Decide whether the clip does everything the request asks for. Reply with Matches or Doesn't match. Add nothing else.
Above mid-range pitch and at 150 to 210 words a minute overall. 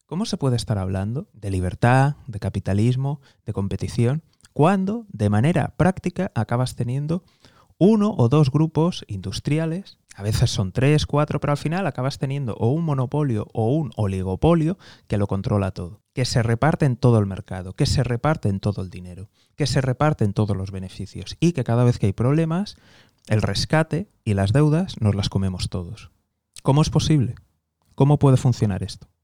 Doesn't match